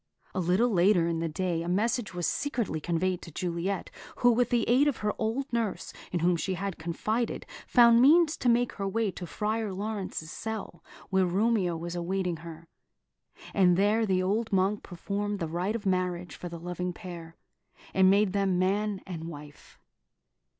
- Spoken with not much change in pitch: No, average, 3.9 semitones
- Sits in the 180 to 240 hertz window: Yes, high, 190 Hz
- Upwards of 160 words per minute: Yes, average, 180 wpm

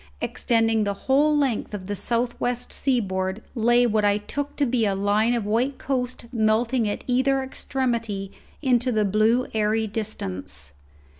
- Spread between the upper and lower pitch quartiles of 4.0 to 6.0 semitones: No, average, 3.2 semitones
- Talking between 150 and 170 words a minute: Yes, average, 155 wpm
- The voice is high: Yes, high, 225 Hz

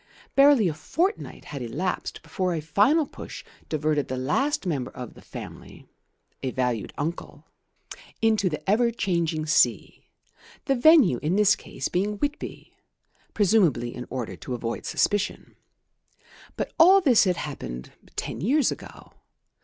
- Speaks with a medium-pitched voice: Yes, medium, 180 Hz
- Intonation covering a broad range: Yes, wide, 8.6 semitones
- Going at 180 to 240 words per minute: No, average, 140 wpm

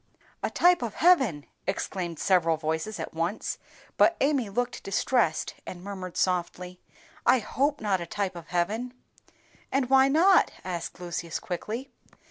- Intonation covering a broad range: Yes, wide, 6.6 semitones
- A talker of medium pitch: No, high, 195 Hz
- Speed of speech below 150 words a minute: Yes, average, 140 wpm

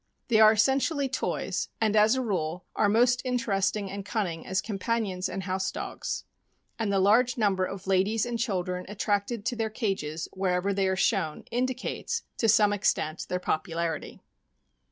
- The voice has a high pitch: Yes, high, 205 Hz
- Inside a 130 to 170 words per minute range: Yes, average, 165 wpm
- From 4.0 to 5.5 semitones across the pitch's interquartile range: No, average, 3.5 semitones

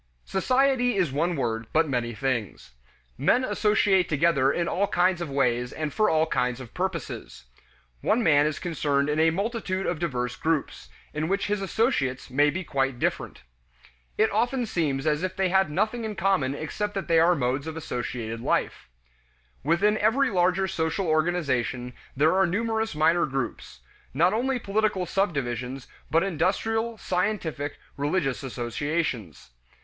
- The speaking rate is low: No, average, 155 wpm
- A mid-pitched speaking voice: Yes, medium, 165 Hz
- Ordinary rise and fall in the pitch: No, wide, 6.2 semitones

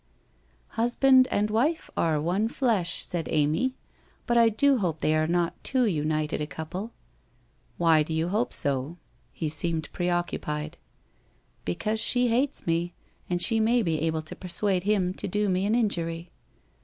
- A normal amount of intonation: No, wide, 5.8 semitones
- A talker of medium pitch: Yes, medium, 175 Hz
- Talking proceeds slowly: No, average, 175 wpm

